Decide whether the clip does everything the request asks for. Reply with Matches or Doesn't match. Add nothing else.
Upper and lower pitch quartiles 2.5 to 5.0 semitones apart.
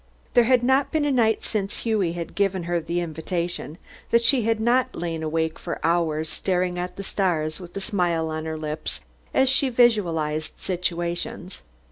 Doesn't match